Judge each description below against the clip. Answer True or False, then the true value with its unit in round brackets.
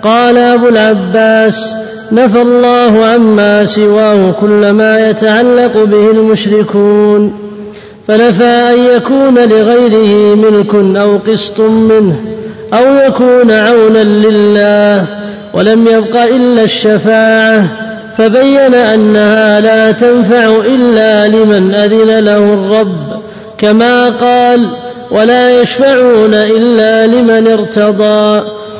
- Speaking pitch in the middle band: False (220 Hz)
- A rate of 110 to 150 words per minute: False (90 wpm)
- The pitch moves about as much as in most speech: False (2.1 semitones)